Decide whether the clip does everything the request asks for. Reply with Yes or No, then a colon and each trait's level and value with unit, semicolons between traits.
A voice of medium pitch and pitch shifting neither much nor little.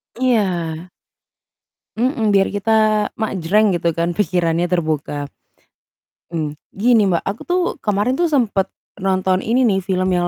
No: high, 195 Hz; average, 4.0 semitones